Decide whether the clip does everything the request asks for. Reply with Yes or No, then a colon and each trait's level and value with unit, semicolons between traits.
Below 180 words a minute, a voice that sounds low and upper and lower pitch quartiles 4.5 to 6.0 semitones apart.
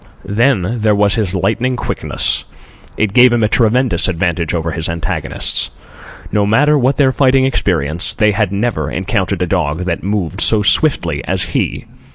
Yes: average, 165 wpm; low, 105 Hz; wide, 5.5 semitones